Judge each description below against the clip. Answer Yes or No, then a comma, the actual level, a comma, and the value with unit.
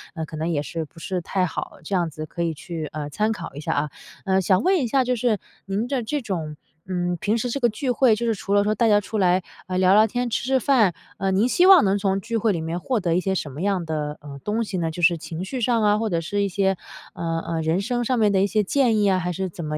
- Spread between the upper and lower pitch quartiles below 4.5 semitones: No, average, 4.8 semitones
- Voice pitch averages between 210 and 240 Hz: No, high, 195 Hz